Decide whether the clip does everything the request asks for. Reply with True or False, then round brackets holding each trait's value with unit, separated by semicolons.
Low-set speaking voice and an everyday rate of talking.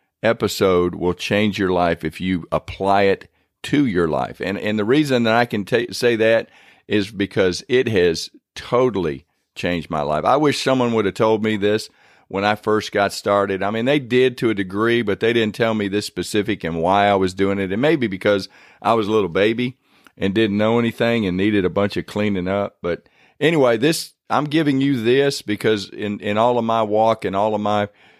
False (105 Hz; 215 wpm)